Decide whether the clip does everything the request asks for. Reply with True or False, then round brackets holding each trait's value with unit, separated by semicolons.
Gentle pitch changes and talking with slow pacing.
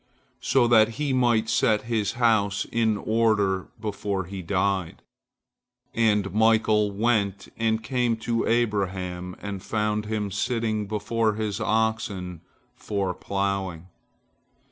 True (2.3 semitones; 115 wpm)